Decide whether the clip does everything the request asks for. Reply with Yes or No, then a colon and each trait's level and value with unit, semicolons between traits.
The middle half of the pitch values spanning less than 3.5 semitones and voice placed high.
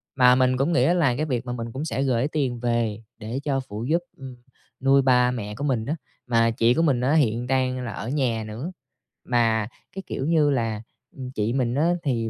No: average, 3.0 semitones; low, 125 Hz